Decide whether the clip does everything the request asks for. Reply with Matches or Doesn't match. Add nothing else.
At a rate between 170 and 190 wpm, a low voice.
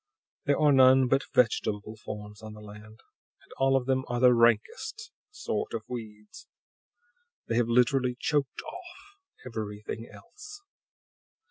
Doesn't match